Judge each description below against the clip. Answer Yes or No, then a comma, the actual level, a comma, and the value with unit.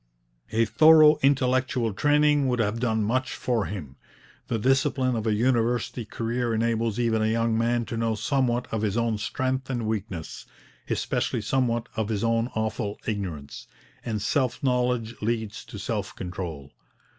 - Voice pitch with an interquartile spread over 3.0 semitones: No, narrow, 2.6 semitones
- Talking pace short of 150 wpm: No, average, 155 wpm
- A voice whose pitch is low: Yes, low, 115 Hz